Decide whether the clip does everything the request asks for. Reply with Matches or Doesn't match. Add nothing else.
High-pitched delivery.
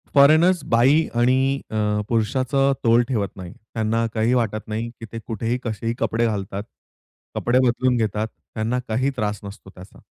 Doesn't match